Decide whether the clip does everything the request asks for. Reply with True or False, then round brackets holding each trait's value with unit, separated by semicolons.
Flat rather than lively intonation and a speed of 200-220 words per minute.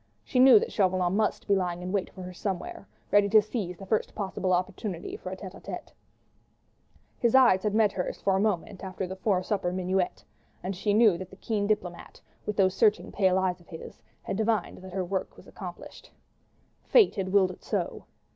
True (2.3 semitones; 205 wpm)